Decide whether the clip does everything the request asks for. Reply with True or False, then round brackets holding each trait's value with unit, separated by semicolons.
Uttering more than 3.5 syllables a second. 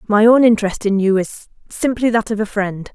True (5.3 syllables/s)